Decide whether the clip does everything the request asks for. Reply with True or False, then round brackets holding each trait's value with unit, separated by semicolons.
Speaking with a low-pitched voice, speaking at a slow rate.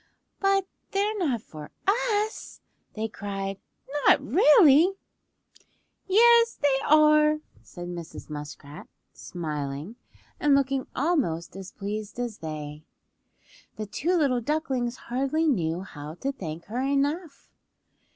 False (255 Hz; 110 wpm)